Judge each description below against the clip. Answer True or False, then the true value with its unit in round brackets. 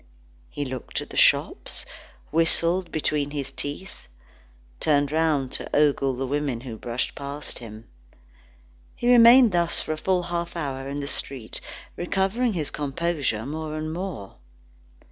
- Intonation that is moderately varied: True (3.9 semitones)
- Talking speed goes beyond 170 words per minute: False (145 wpm)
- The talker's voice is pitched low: False (150 Hz)